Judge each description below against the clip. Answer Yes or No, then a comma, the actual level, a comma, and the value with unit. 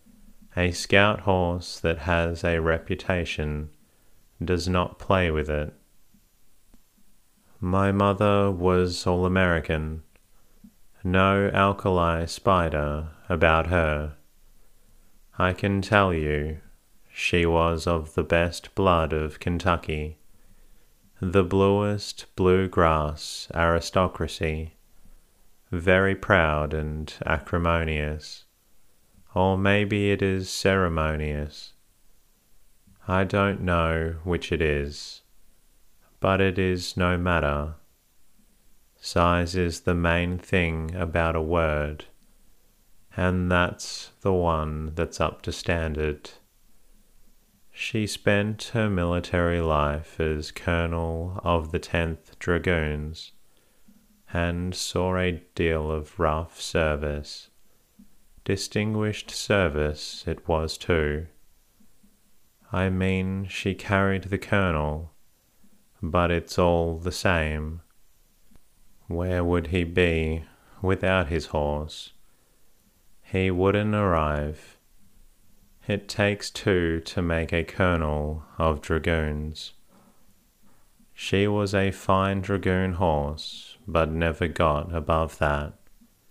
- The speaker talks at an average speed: No, slow, 95 wpm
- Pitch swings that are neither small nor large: Yes, average, 3.4 semitones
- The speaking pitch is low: Yes, very low, 85 Hz